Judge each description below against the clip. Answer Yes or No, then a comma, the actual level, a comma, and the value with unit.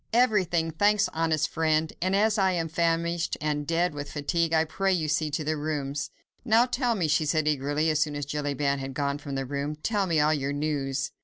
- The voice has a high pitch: No, medium, 155 Hz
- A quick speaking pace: Yes, fast, 215 wpm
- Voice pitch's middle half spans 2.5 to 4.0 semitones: Yes, average, 2.8 semitones